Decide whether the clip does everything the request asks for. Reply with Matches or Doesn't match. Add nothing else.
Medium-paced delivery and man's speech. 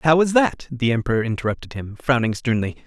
Matches